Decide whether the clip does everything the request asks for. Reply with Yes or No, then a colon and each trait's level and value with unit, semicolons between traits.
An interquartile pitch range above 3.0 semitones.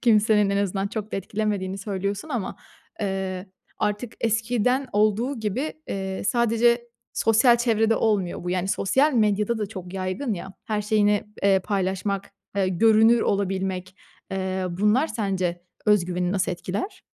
No: average, 2.7 semitones